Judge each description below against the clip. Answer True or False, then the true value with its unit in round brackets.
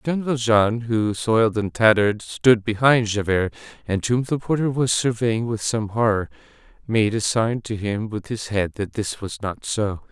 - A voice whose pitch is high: False (110 Hz)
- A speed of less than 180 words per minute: False (185 wpm)